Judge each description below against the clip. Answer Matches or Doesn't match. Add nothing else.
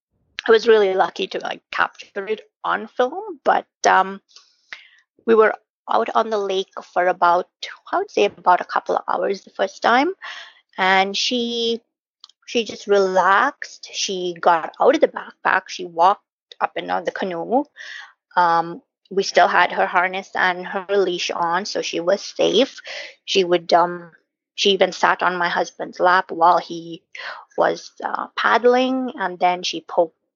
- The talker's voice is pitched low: Doesn't match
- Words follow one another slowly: Doesn't match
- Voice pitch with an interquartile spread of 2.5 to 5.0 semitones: Doesn't match